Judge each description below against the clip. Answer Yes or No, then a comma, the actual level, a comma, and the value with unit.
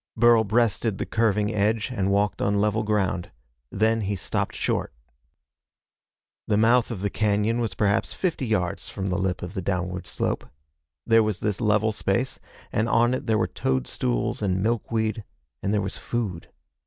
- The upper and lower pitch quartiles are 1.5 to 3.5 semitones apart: Yes, narrow, 2.6 semitones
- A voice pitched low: Yes, low, 105 Hz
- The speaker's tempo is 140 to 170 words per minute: Yes, average, 165 wpm